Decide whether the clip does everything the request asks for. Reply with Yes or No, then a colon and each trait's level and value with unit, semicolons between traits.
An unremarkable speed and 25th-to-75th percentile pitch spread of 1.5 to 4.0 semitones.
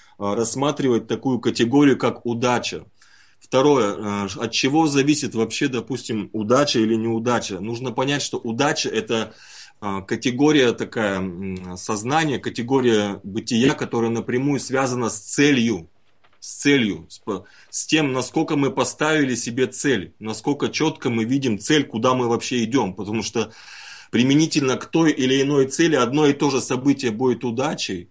Yes: average, 130 wpm; average, 3.7 semitones